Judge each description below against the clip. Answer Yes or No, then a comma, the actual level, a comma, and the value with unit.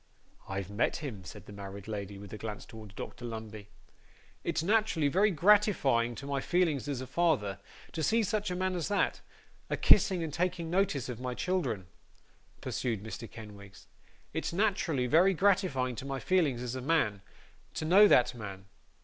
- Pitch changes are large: Yes, wide, 8.6 semitones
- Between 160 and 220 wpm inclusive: Yes, average, 175 wpm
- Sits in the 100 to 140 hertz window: Yes, low, 135 Hz